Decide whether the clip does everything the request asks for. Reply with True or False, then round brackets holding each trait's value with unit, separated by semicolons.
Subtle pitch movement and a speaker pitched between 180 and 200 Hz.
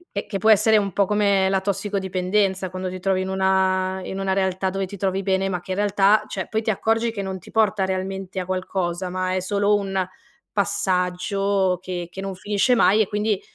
True (1.4 semitones; 190 Hz)